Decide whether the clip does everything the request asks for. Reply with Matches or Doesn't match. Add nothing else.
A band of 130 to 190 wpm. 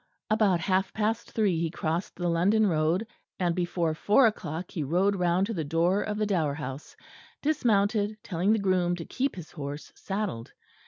Matches